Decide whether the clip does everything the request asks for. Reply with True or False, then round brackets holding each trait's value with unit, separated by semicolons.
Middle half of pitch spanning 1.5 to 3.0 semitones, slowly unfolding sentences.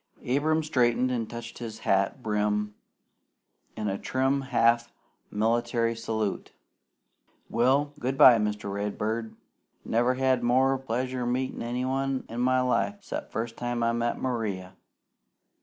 True (2.6 semitones; 125 wpm)